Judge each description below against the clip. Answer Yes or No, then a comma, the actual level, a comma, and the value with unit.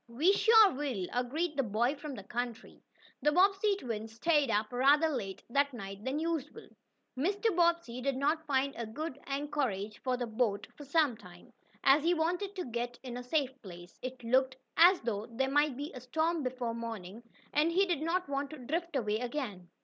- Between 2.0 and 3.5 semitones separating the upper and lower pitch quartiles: No, average, 5.2 semitones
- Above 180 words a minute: Yes, average, 190 wpm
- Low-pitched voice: No, very high, 270 Hz